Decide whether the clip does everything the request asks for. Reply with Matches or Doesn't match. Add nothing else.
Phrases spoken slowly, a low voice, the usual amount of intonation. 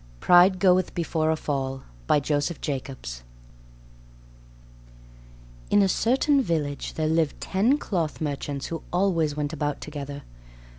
Doesn't match